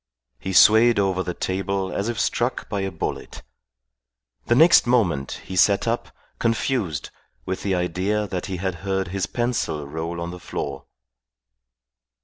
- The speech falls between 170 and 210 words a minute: No, average, 150 wpm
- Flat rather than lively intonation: No, average, 3.0 semitones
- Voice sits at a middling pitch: No, very low, 95 Hz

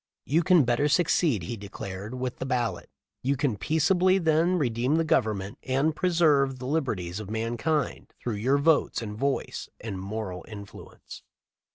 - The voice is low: Yes, low, 130 Hz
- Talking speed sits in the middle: Yes, average, 160 wpm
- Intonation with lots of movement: Yes, wide, 6.3 semitones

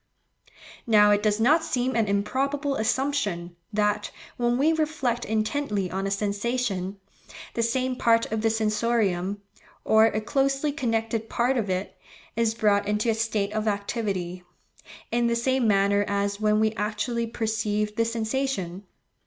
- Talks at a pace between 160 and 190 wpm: No, average, 145 wpm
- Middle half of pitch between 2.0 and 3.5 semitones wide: Yes, average, 2.8 semitones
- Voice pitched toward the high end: Yes, high, 220 Hz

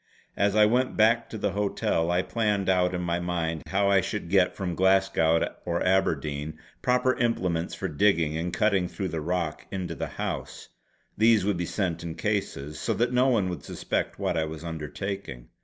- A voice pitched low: Yes, very low, 90 Hz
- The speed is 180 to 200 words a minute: Yes, average, 190 wpm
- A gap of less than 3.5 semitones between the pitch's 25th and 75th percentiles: No, average, 3.8 semitones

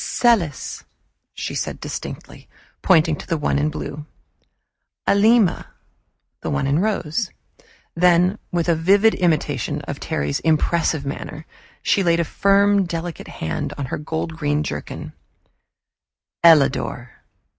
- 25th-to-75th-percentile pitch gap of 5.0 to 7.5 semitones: No, average, 3.9 semitones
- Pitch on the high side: No, medium, 165 Hz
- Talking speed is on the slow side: Yes, slow, 125 wpm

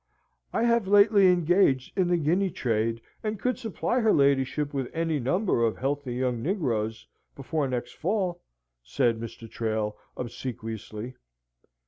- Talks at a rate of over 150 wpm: No, slow, 135 wpm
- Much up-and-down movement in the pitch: Yes, wide, 7.9 semitones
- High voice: No, medium, 140 Hz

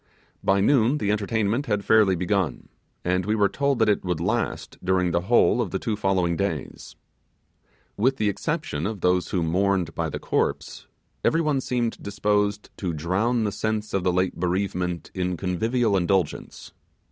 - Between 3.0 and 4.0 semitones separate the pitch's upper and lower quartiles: Yes, average, 3.4 semitones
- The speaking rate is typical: Yes, average, 170 wpm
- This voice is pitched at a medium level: No, low, 100 Hz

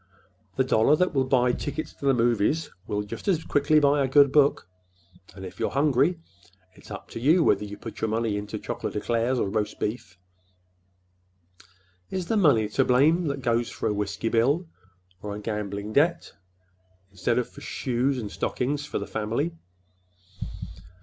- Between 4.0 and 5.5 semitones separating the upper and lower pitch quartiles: Yes, average, 5.2 semitones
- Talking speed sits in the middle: Yes, average, 170 wpm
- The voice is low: Yes, low, 125 Hz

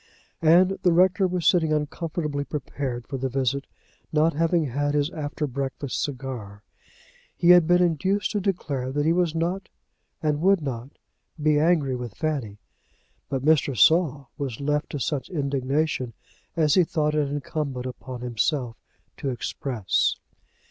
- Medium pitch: Yes, medium, 145 Hz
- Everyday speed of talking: Yes, average, 150 wpm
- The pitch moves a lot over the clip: No, average, 3.8 semitones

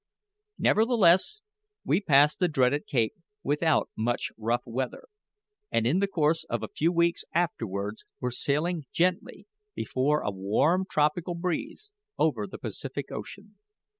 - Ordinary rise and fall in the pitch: No, wide, 5.9 semitones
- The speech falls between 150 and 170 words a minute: No, slow, 135 wpm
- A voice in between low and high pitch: Yes, medium, 150 Hz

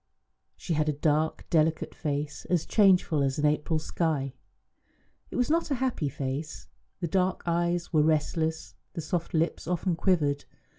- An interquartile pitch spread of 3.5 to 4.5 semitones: No, average, 2.8 semitones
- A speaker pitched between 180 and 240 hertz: No, medium, 160 Hz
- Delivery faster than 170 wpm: No, average, 155 wpm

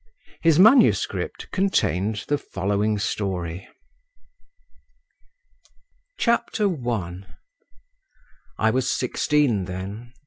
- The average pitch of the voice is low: Yes, low, 110 Hz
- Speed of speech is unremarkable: No, slow, 65 wpm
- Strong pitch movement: Yes, wide, 7.4 semitones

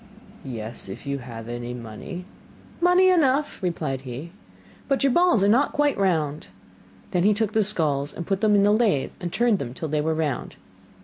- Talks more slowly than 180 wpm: No, average, 190 wpm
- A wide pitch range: Yes, wide, 8.2 semitones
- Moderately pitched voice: Yes, medium, 175 Hz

